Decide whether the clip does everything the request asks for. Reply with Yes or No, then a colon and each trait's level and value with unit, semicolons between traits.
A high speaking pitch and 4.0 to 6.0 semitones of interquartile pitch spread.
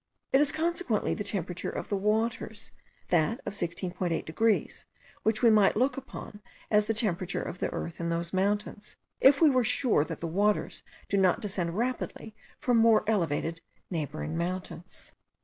Yes: high, 205 Hz; average, 4.5 semitones